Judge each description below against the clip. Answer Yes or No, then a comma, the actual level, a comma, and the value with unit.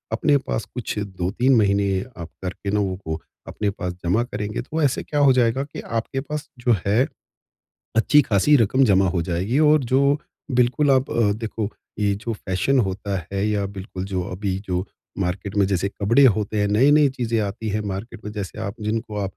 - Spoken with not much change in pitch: No, average, 3.9 semitones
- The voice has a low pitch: Yes, low, 105 Hz